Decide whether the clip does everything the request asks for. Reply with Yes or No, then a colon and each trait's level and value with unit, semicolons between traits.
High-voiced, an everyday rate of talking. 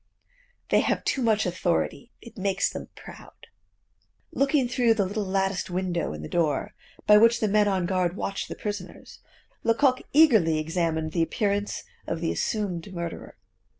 Yes: high, 195 Hz; average, 155 wpm